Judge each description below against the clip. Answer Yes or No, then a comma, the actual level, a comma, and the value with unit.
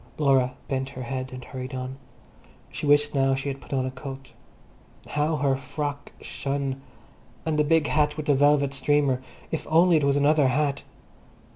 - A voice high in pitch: No, medium, 140 Hz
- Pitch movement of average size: No, narrow, 1.9 semitones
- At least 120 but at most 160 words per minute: No, average, 170 wpm